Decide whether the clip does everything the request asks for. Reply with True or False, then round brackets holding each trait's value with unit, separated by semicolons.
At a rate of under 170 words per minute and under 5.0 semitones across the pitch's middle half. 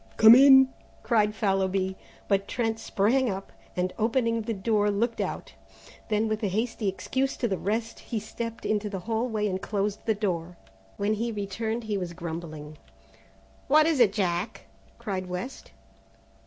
True (160 wpm; 3.1 semitones)